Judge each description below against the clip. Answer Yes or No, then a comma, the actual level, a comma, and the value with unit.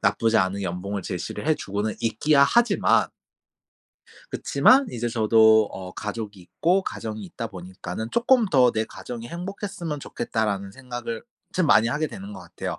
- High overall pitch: No, low, 115 Hz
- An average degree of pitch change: No, wide, 7.2 semitones